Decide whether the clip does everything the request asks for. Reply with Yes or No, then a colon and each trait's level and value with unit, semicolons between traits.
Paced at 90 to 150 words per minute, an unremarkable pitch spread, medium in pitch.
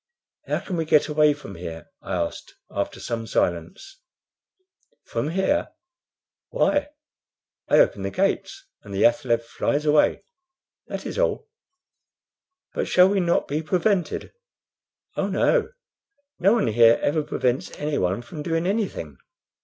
No: slow, 135 wpm; wide, 8.4 semitones; medium, 150 Hz